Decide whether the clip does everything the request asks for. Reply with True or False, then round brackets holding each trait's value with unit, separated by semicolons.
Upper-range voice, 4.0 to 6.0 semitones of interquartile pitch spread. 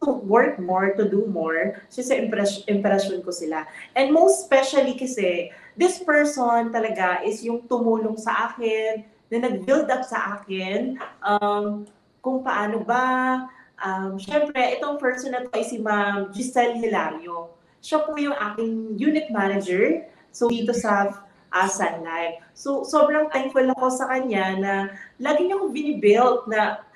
True (225 Hz; 4.4 semitones)